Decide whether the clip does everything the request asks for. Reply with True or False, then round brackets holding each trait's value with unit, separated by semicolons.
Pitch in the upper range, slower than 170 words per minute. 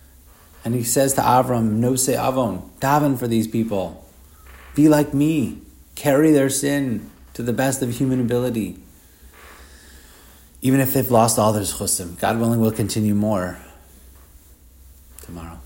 False (105 Hz; 140 wpm)